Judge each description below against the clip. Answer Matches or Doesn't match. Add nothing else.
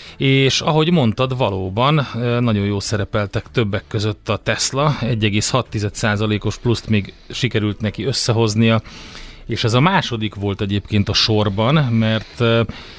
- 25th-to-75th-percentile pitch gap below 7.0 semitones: Matches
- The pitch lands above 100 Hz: Matches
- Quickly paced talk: Doesn't match